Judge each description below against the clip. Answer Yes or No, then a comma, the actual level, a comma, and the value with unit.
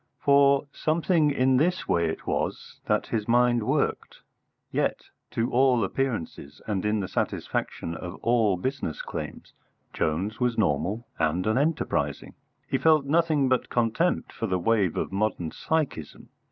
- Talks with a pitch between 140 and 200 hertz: No, low, 115 Hz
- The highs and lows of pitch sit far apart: Yes, wide, 6.5 semitones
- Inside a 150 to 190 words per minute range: No, average, 140 wpm